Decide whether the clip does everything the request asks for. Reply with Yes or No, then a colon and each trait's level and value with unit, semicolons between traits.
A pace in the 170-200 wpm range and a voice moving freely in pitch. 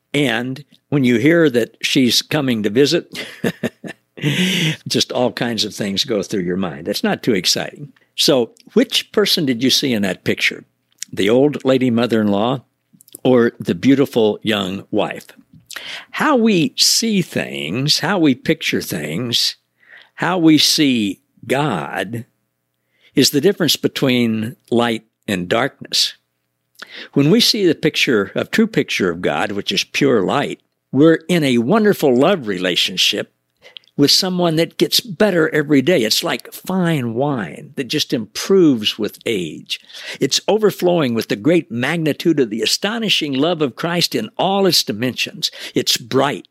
No: average, 150 wpm; wide, 6.6 semitones